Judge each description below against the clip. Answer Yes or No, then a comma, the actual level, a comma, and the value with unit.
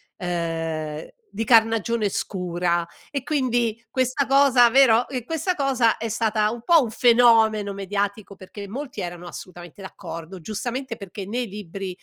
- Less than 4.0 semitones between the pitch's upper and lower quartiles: No, average, 4.7 semitones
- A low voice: No, high, 215 Hz